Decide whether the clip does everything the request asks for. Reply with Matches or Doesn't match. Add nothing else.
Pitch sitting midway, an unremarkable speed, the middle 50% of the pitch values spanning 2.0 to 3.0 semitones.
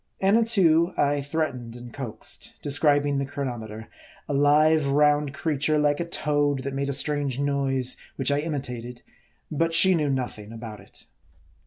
Matches